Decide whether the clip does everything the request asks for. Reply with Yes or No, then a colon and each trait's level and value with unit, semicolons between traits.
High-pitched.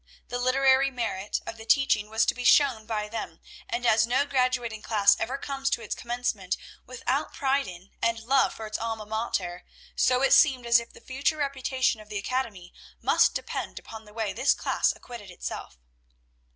Yes: high, 235 Hz